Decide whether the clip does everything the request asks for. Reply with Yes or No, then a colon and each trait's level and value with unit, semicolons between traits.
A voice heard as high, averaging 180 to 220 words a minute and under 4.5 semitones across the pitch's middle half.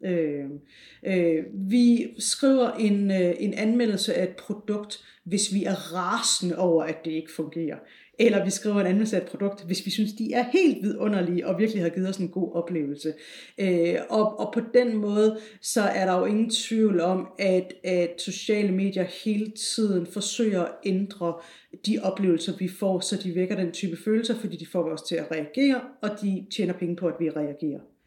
Yes: high, 195 Hz; average, 190 wpm; average, 3.6 semitones